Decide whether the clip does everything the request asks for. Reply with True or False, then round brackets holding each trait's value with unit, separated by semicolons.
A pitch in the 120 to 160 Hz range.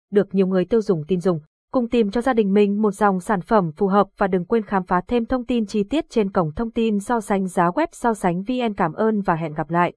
False (205 Hz)